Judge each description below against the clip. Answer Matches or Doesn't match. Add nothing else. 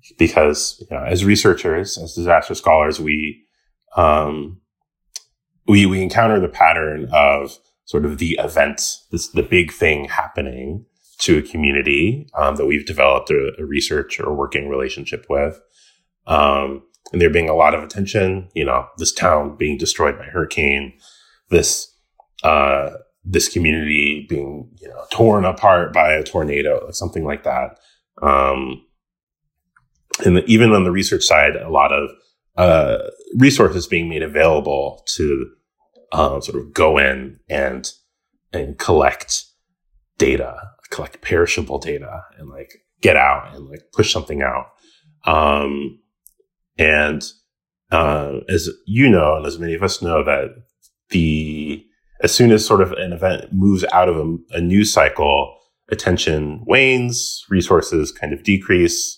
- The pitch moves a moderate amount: Doesn't match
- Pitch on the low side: Matches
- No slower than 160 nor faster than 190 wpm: Doesn't match